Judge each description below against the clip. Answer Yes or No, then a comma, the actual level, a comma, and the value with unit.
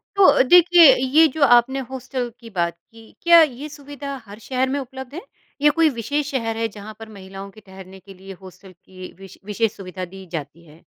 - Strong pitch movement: Yes, wide, 6.6 semitones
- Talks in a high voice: Yes, high, 230 Hz